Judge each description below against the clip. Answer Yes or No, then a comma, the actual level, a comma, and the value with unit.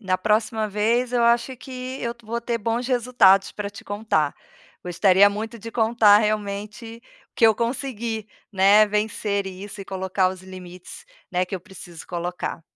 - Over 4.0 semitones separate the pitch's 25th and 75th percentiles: No, average, 3.4 semitones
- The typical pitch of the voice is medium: No, high, 210 Hz